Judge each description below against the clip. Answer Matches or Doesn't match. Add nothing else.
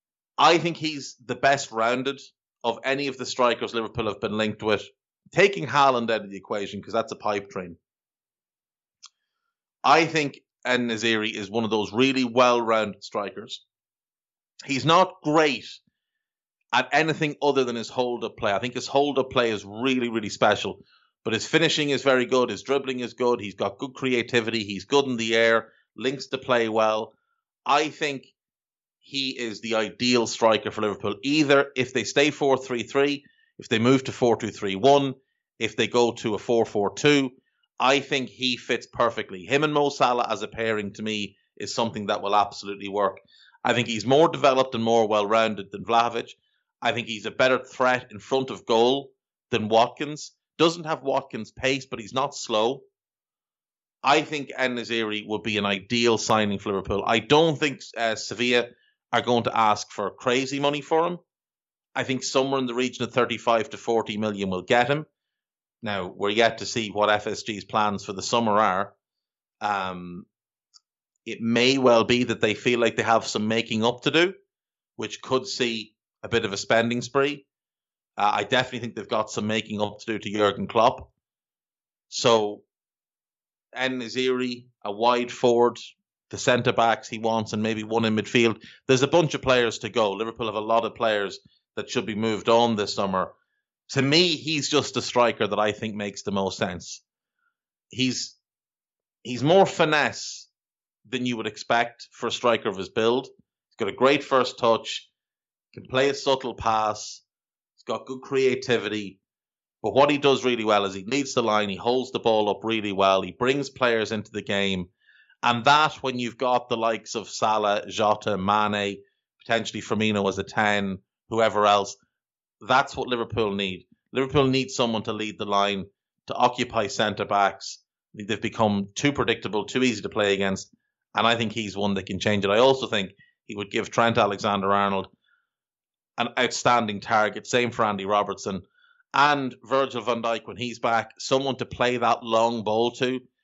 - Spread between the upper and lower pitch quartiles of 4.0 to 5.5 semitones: Doesn't match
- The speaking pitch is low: Matches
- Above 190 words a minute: Doesn't match